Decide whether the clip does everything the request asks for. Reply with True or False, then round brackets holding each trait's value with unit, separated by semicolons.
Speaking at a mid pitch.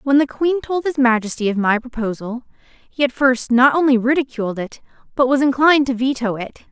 False (255 Hz)